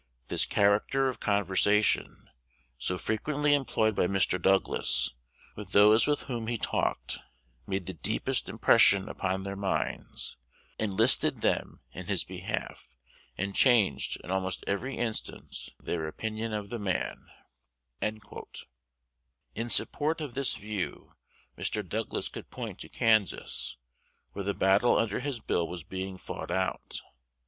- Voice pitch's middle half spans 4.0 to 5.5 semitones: No, average, 3.3 semitones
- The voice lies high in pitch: No, low, 100 Hz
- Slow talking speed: Yes, slow, 130 wpm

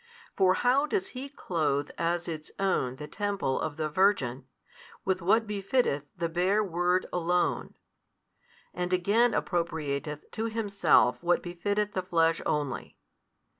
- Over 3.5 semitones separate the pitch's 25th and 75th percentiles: Yes, average, 4.4 semitones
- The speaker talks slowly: Yes, slow, 130 wpm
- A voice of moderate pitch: Yes, medium, 180 Hz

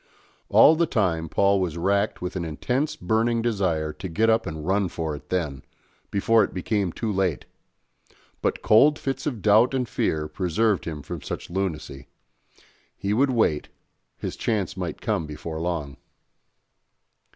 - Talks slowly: No, average, 155 wpm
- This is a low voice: Yes, very low, 95 Hz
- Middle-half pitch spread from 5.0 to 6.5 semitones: Yes, wide, 5.5 semitones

